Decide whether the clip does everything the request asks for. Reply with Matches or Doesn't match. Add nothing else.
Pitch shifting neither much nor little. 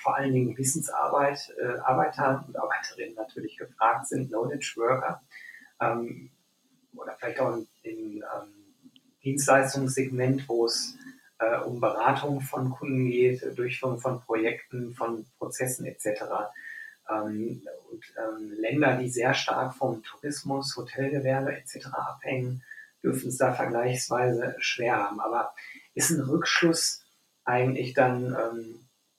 Matches